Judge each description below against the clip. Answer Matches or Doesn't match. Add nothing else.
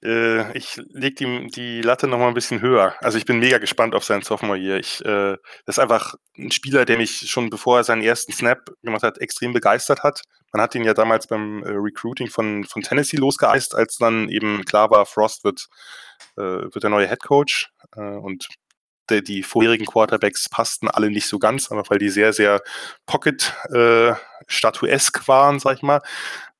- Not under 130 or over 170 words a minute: Doesn't match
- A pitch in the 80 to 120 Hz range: Matches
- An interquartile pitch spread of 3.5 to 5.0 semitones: Doesn't match